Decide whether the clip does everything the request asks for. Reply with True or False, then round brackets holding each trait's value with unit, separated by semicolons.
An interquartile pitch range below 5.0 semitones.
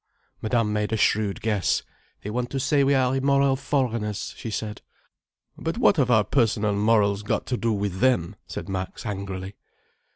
True (4.1 semitones)